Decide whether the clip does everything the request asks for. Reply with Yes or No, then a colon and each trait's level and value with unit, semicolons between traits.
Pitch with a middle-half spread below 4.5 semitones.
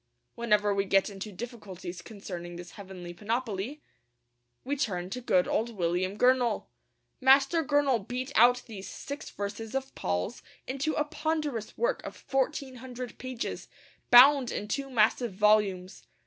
No: average, 5.2 semitones